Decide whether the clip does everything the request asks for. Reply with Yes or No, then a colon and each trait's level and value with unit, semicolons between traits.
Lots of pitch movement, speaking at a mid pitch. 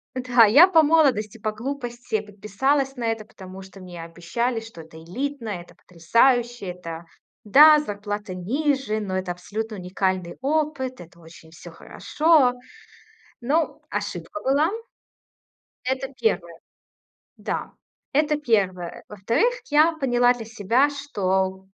No: wide, 6.3 semitones; high, 225 Hz